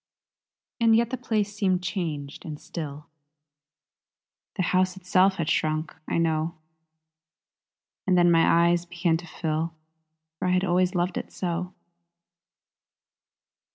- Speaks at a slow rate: Yes, slow, 125 wpm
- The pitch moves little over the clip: Yes, narrow, 2.2 semitones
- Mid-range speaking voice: Yes, medium, 175 Hz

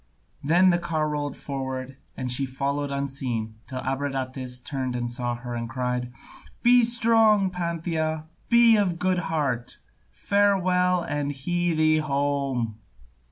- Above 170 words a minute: No, slow, 135 wpm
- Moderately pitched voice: Yes, medium, 145 Hz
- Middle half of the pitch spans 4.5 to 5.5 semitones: Yes, average, 5.2 semitones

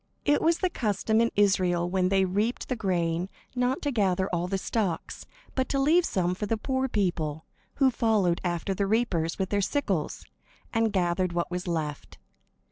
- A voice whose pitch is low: No, high, 195 Hz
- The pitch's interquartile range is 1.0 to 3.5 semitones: No, average, 4.6 semitones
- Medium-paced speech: Yes, average, 180 wpm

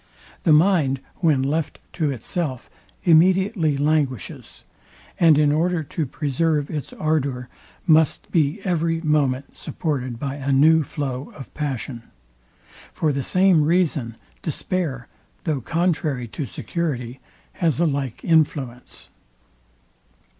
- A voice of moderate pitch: Yes, medium, 150 Hz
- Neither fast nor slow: No, slow, 115 wpm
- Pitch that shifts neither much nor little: Yes, average, 3.5 semitones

